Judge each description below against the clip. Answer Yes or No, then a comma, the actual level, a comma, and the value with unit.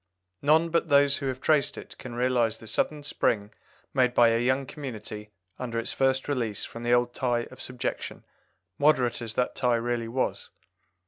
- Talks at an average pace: Yes, average, 180 wpm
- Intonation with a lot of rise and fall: No, average, 2.7 semitones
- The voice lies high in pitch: No, low, 125 Hz